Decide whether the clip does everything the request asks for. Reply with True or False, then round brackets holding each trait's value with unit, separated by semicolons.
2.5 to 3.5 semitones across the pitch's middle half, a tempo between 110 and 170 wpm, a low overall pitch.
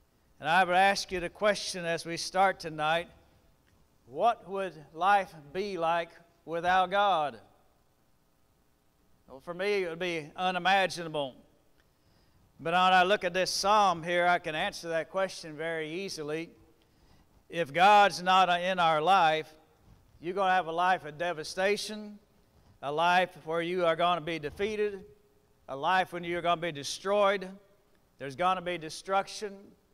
False (3.1 semitones; 150 wpm; 175 Hz)